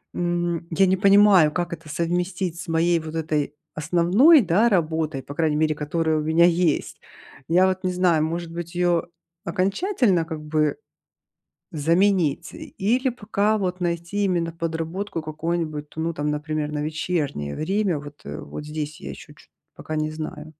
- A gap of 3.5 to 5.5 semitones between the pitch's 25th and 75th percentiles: No, average, 2.8 semitones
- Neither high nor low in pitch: Yes, medium, 165 Hz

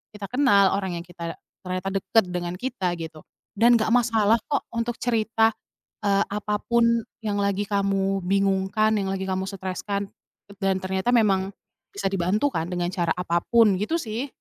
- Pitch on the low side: No, high, 200 Hz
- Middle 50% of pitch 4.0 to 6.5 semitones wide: No, average, 2.8 semitones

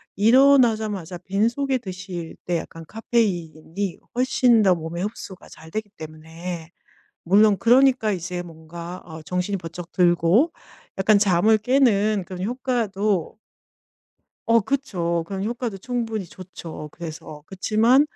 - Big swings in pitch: No, average, 4.7 semitones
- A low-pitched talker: No, high, 195 Hz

